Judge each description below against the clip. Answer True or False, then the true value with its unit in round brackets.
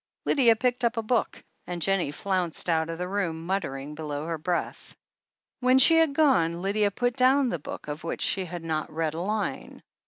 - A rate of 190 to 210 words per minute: True (195 wpm)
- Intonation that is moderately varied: False (6.4 semitones)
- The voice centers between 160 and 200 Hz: True (185 Hz)